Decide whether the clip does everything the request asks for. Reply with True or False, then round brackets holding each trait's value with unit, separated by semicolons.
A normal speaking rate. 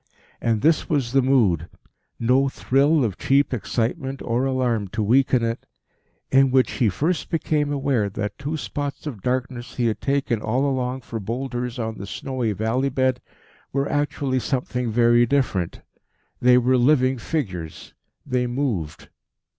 True (150 wpm)